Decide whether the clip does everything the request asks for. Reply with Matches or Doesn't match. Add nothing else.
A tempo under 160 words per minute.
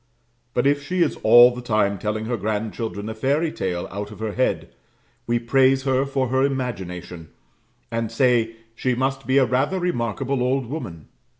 Doesn't match